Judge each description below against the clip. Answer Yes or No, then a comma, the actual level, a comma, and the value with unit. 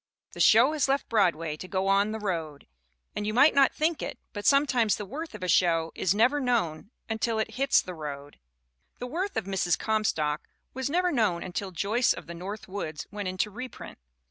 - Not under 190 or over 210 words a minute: Yes, average, 200 wpm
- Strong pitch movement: Yes, wide, 6.0 semitones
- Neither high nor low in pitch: No, high, 205 Hz